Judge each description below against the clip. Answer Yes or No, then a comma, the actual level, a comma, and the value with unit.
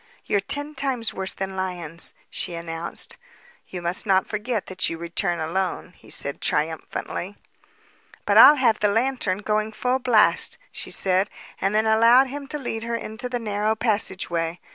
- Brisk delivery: No, average, 165 wpm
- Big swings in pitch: No, average, 4.2 semitones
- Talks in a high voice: Yes, high, 205 Hz